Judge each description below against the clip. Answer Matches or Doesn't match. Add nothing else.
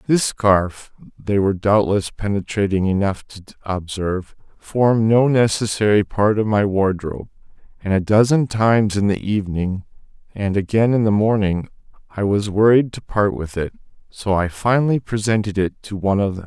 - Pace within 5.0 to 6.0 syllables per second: Matches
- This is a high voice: Doesn't match